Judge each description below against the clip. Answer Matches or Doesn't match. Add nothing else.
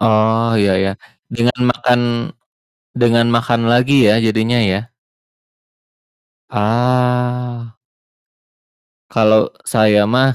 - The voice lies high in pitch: Doesn't match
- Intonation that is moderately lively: Doesn't match